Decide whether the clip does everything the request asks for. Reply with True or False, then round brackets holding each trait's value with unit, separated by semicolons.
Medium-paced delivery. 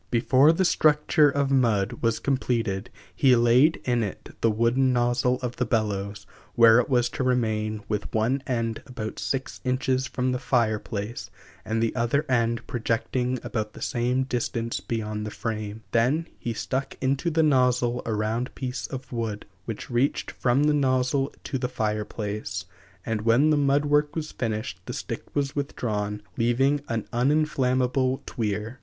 True (165 wpm)